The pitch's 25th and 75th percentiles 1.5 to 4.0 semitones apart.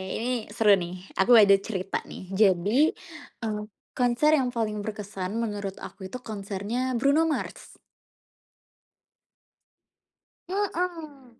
No: average, 4.5 semitones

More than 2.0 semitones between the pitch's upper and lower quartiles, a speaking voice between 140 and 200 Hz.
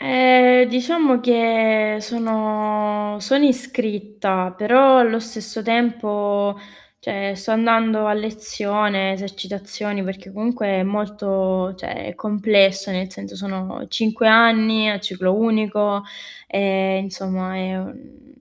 No: average, 2.7 semitones; high, 210 Hz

